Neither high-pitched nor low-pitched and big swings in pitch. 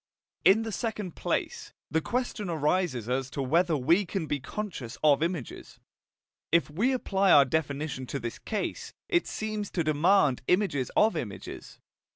Yes: medium, 165 Hz; wide, 6.2 semitones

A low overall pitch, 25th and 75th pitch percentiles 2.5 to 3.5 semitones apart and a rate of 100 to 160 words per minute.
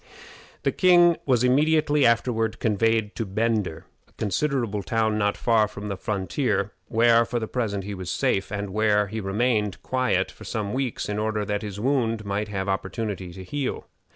No: low, 110 Hz; average, 2.9 semitones; average, 175 wpm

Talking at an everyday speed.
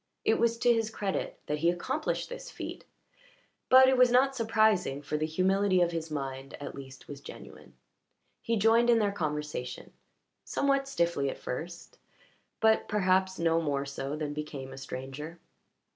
Yes: average, 160 wpm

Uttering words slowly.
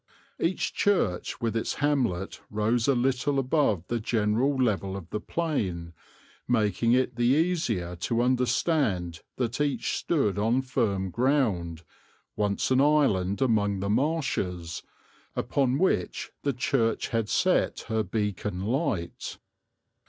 Yes: slow, 125 wpm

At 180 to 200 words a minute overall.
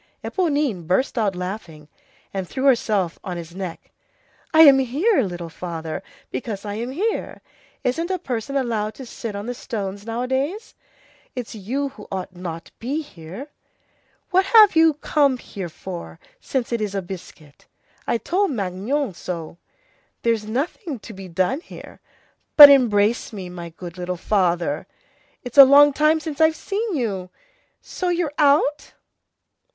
No: average, 150 wpm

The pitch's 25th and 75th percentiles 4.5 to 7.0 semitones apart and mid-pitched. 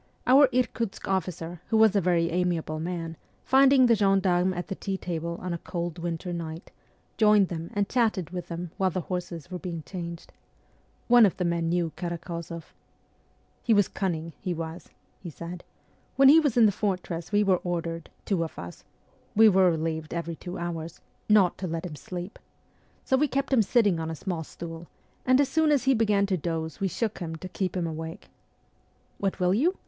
No: average, 3.6 semitones; medium, 180 Hz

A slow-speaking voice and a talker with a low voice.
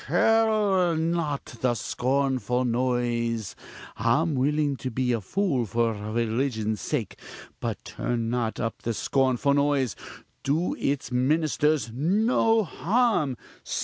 Yes: slow, 115 wpm; low, 130 Hz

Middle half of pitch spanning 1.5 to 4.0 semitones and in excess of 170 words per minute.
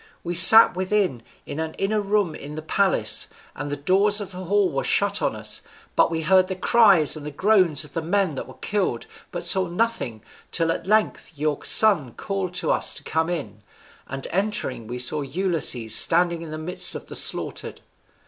No: average, 4.6 semitones; average, 195 wpm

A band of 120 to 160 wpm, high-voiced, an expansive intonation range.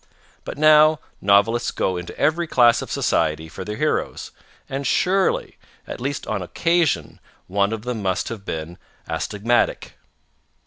No: average, 140 wpm; low, 115 Hz; wide, 7.6 semitones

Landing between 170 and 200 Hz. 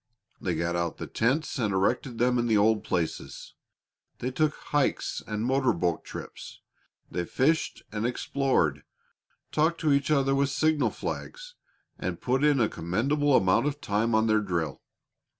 No: low, 120 Hz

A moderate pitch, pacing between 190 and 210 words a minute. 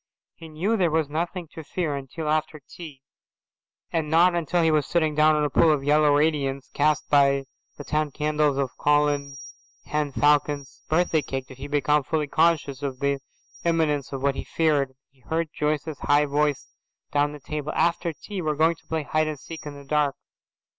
Yes: medium, 150 Hz; average, 195 wpm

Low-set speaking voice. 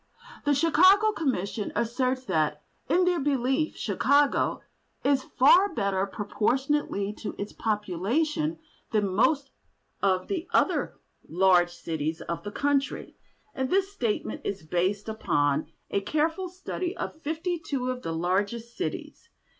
No: very high, 250 Hz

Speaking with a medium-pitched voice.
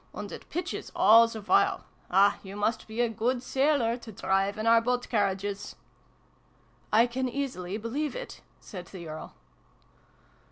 No: high, 225 Hz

